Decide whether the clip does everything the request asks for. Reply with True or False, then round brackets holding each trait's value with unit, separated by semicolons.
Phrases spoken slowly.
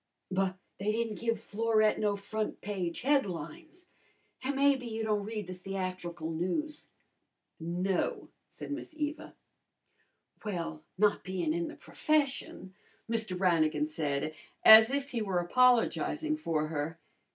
True (130 wpm)